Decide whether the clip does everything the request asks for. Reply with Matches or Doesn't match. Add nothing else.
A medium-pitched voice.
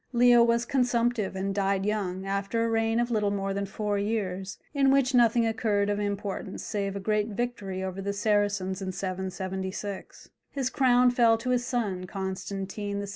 Doesn't match